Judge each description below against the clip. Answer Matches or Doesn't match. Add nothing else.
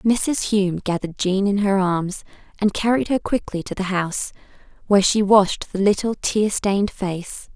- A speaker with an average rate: Matches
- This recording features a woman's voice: Matches